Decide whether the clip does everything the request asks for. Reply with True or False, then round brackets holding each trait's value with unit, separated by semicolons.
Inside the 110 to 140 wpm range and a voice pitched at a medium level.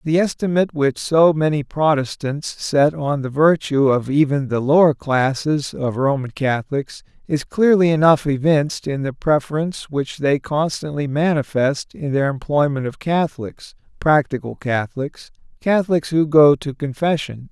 True (135 wpm; 145 Hz)